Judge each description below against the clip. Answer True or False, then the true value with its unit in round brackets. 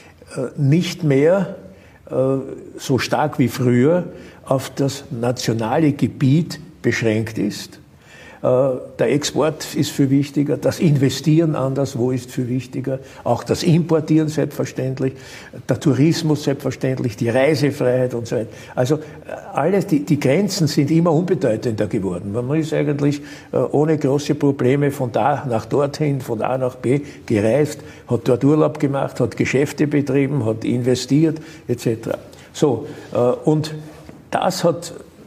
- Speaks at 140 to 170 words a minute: False (130 wpm)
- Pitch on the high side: False (140 Hz)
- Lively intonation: False (3.3 semitones)